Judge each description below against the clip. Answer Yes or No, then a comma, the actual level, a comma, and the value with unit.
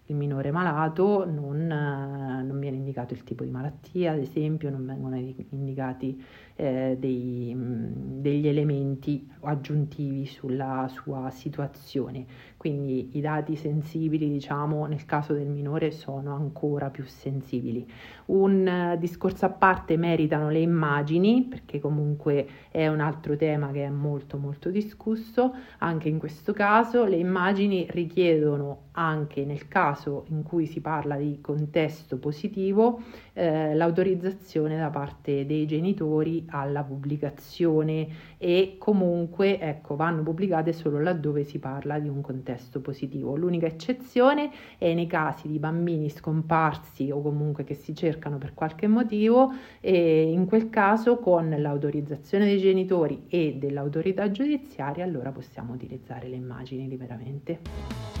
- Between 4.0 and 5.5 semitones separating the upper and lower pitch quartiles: No, average, 3.3 semitones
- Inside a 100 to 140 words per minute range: Yes, average, 130 wpm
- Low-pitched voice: No, medium, 150 Hz